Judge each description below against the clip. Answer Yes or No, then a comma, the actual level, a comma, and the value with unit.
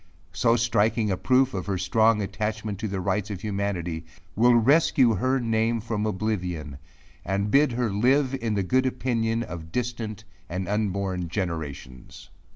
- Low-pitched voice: Yes, low, 105 Hz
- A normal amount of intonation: Yes, average, 3.8 semitones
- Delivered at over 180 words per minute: No, average, 155 wpm